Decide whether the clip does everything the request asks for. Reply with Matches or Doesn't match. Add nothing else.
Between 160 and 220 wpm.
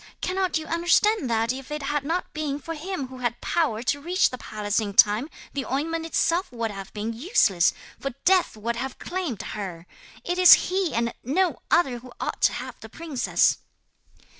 Matches